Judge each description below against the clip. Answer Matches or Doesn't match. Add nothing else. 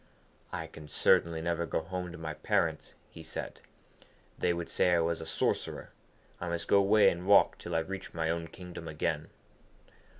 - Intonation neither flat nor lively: Doesn't match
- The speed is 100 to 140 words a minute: Doesn't match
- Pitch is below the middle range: Matches